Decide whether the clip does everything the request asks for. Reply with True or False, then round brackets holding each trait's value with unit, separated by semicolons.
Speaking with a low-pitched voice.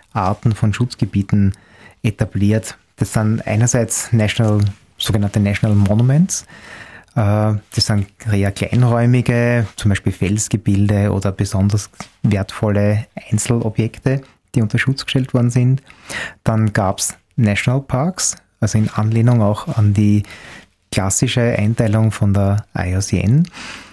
True (110 Hz)